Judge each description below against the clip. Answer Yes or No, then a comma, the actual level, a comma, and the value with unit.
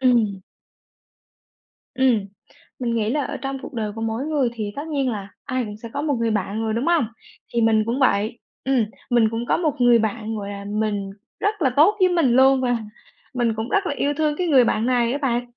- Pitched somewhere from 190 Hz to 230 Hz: No, high, 240 Hz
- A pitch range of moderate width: Yes, average, 3.8 semitones